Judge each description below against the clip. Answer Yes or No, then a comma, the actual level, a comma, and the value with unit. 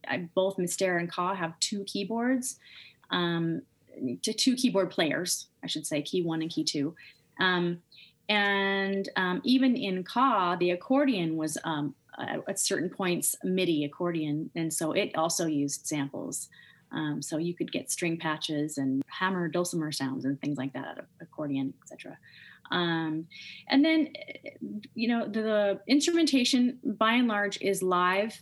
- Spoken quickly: No, average, 160 wpm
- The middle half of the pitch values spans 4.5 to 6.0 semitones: Yes, average, 5.1 semitones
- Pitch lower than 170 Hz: No, medium, 180 Hz